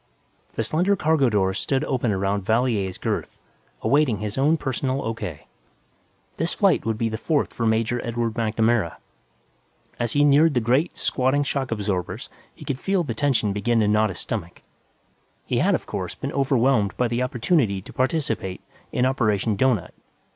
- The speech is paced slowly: No, average, 165 wpm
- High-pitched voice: No, low, 120 Hz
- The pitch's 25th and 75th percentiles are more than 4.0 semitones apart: Yes, average, 4.4 semitones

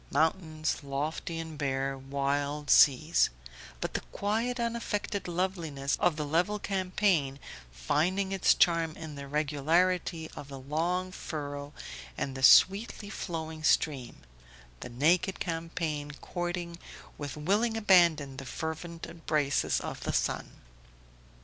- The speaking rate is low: Yes, slow, 120 wpm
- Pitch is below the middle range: No, medium, 160 Hz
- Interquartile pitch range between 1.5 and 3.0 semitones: No, average, 4.0 semitones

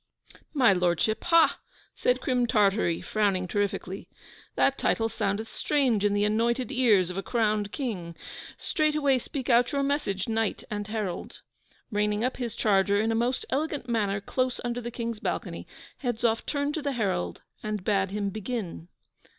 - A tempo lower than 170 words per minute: Yes, average, 160 wpm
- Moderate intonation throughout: Yes, average, 3.9 semitones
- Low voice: No, high, 220 Hz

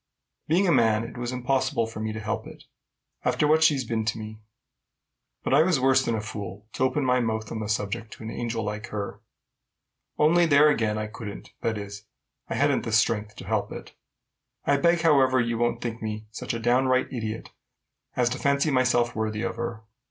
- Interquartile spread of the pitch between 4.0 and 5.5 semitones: No, average, 3.3 semitones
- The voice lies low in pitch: Yes, low, 115 Hz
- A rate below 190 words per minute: No, fast, 205 wpm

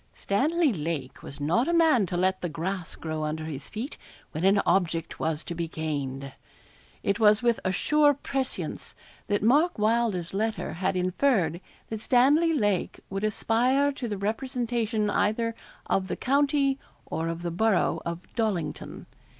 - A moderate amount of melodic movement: No, wide, 6.4 semitones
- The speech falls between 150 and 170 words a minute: Yes, average, 160 wpm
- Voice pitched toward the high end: Yes, high, 205 Hz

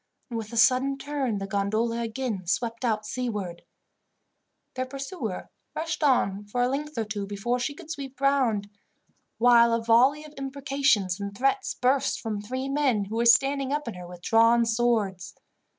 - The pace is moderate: Yes, average, 170 wpm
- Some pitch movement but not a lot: Yes, average, 4.4 semitones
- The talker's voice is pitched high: Yes, high, 235 Hz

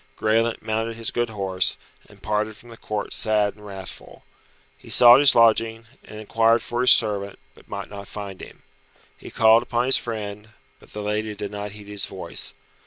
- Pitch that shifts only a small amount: Yes, narrow, 1.9 semitones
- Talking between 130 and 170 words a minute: No, average, 185 wpm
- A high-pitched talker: No, low, 110 Hz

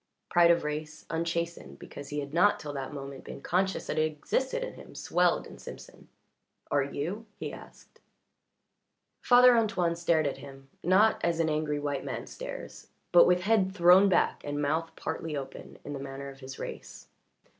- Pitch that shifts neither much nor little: Yes, average, 4.0 semitones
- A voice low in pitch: No, medium, 160 Hz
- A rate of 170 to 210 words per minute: Yes, average, 175 wpm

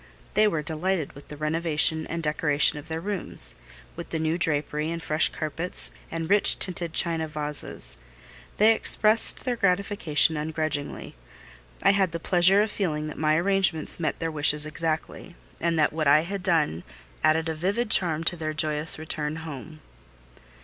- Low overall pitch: No, medium, 160 Hz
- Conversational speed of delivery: Yes, average, 165 wpm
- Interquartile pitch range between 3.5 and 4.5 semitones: No, narrow, 2.6 semitones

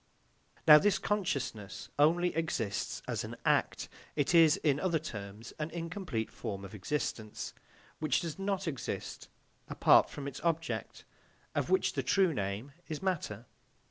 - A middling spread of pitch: No, wide, 7.5 semitones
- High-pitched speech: No, medium, 150 Hz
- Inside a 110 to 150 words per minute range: Yes, average, 140 wpm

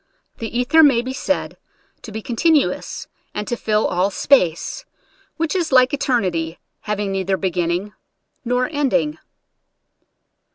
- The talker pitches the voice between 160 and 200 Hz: No, high, 225 Hz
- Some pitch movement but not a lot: No, wide, 5.7 semitones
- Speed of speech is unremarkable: No, slow, 130 wpm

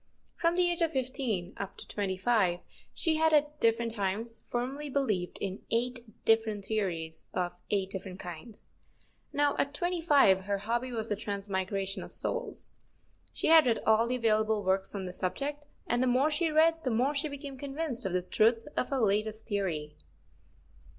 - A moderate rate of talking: Yes, average, 175 wpm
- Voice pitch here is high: Yes, high, 225 Hz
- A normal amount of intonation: No, wide, 6.2 semitones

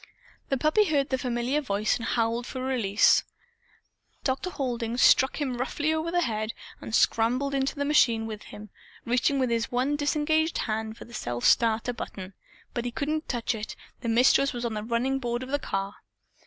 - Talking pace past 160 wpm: Yes, average, 185 wpm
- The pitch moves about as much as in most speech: Yes, average, 3.5 semitones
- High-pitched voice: Yes, high, 245 Hz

